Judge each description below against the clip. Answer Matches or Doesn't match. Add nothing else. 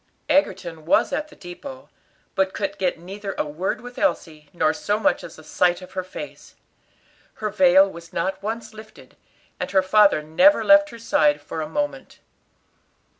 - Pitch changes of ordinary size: Matches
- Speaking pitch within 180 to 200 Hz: Matches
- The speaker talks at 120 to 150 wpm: Doesn't match